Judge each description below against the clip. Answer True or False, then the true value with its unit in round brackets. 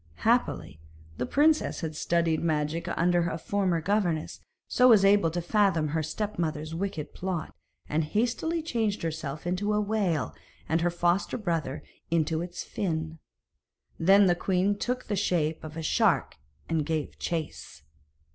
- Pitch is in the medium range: True (170 Hz)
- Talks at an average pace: True (150 wpm)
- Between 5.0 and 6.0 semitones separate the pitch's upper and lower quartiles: False (4.1 semitones)